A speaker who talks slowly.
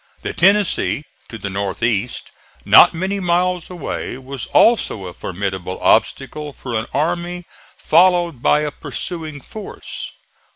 Yes: slow, 130 wpm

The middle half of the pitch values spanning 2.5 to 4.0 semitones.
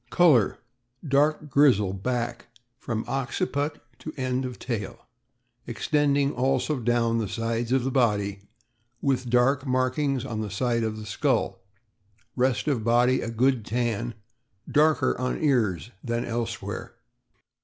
Yes: average, 2.8 semitones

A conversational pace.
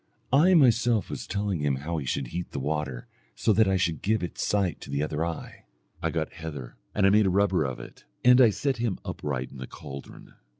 No: fast, 225 wpm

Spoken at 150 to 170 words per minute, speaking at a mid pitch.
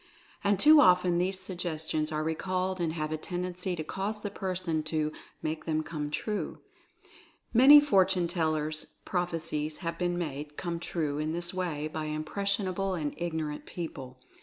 Yes: average, 160 wpm; medium, 170 Hz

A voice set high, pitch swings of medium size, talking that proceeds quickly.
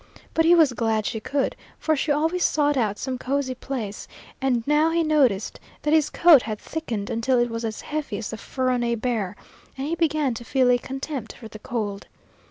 Yes: very high, 255 Hz; average, 4.8 semitones; fast, 210 wpm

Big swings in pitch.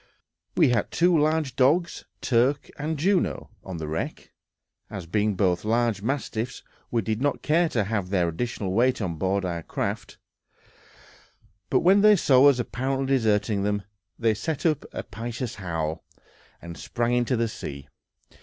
Yes: wide, 5.9 semitones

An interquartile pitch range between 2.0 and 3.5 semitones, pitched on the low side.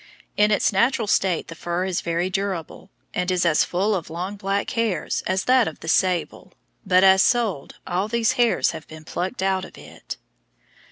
No: average, 2.9 semitones; high, 190 Hz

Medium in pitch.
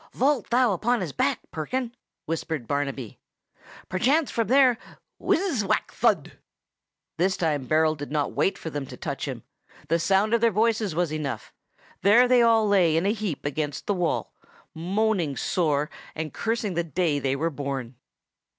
Yes: medium, 180 Hz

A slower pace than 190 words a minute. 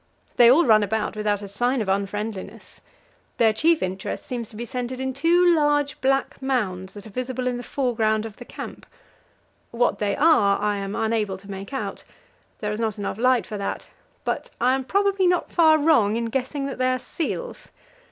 No: average, 195 wpm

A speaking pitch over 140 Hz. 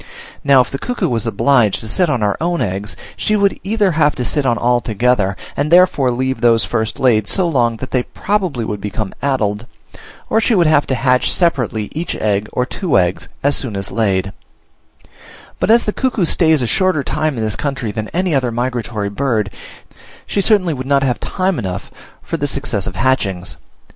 No: low, 130 Hz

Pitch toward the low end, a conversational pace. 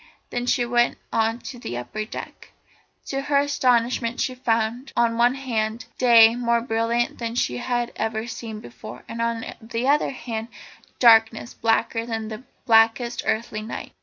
No: high, 235 Hz; average, 165 wpm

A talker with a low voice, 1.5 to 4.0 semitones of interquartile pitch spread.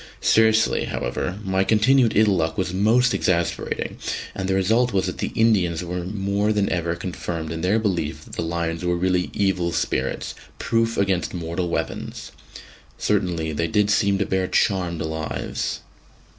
Yes: very low, 95 Hz; average, 3.4 semitones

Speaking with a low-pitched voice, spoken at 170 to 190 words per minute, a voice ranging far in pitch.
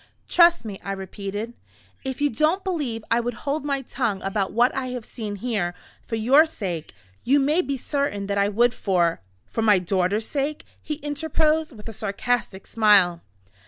No: high, 225 Hz; average, 175 wpm; wide, 5.9 semitones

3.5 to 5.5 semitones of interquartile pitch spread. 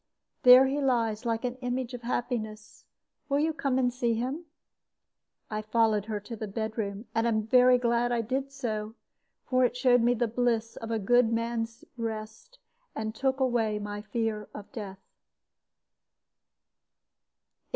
No: narrow, 2.4 semitones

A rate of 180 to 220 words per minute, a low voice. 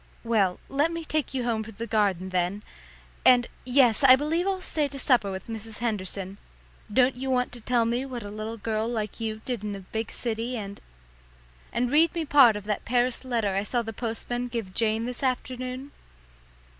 No: average, 195 wpm; high, 235 Hz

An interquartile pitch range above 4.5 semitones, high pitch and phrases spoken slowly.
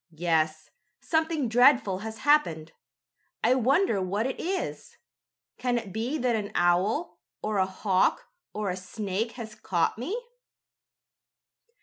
Yes: wide, 5.5 semitones; high, 215 Hz; slow, 125 wpm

